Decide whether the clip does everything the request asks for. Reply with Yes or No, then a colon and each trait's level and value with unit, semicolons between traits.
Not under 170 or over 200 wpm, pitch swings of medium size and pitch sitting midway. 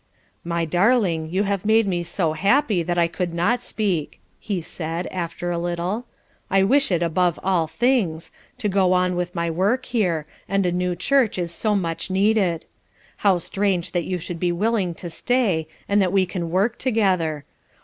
Yes: average, 180 wpm; average, 3.2 semitones; medium, 180 Hz